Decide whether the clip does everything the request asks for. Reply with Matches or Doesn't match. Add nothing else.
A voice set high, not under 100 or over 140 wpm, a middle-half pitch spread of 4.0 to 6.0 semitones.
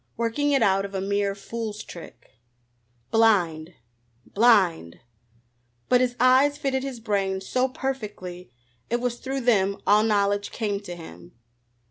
Matches